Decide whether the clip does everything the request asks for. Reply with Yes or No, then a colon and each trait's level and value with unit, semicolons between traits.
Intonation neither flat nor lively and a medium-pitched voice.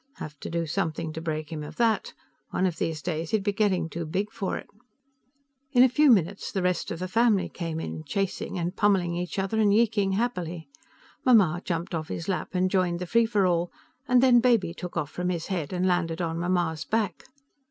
Yes: average, 3.6 semitones; medium, 180 Hz